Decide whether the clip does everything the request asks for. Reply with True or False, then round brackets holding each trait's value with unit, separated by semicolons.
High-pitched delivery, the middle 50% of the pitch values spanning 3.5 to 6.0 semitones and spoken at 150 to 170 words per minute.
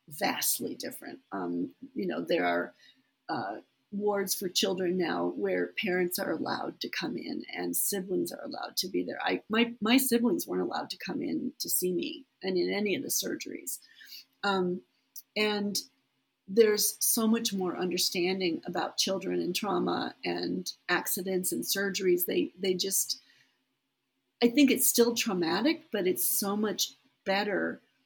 True (195 Hz; 3.8 semitones; 155 wpm)